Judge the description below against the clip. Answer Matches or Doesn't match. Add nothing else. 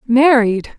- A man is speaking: Doesn't match